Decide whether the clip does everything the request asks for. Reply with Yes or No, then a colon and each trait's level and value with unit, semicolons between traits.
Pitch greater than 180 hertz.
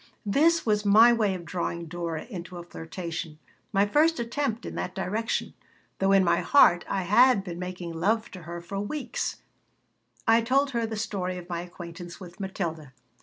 Yes: high, 190 Hz